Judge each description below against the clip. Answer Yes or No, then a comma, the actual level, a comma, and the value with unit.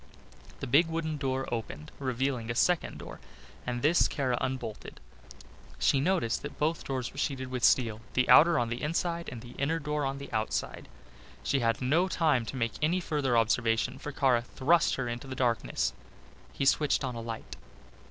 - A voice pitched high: No, low, 130 Hz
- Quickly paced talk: No, average, 180 wpm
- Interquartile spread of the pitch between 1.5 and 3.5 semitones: No, average, 3.9 semitones